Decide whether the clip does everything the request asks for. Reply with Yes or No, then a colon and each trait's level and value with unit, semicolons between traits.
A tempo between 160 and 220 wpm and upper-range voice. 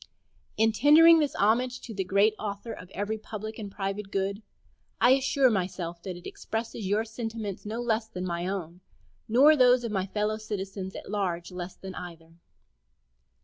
Yes: average, 170 wpm; high, 210 Hz